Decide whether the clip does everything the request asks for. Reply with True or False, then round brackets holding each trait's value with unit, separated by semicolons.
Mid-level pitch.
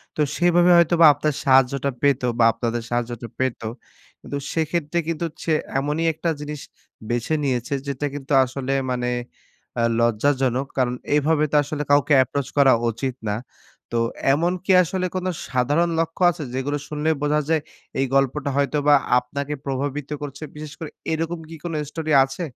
True (145 Hz)